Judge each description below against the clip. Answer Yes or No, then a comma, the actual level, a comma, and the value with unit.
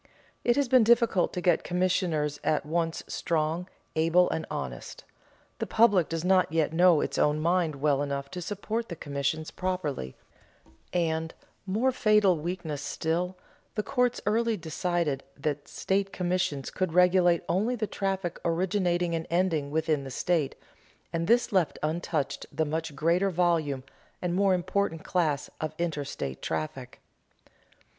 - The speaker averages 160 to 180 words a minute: No, average, 145 wpm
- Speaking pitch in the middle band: Yes, medium, 170 Hz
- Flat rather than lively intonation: No, average, 3.3 semitones